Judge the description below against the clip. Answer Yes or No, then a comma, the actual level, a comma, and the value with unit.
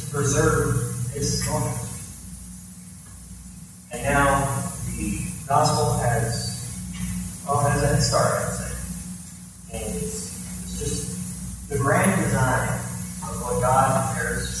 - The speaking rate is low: Yes, slow, 105 wpm